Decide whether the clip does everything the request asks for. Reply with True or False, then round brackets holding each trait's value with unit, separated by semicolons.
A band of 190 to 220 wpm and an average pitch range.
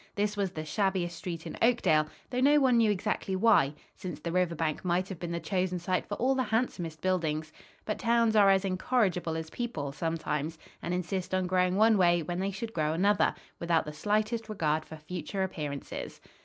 True (195 wpm; 4.3 semitones)